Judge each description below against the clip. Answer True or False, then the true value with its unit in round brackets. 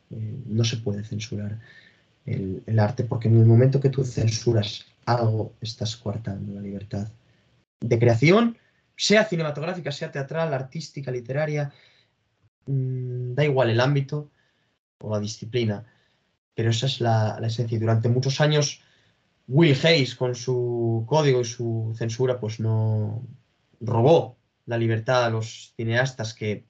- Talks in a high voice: False (120 Hz)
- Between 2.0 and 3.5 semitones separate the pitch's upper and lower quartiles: True (3.2 semitones)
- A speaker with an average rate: True (140 wpm)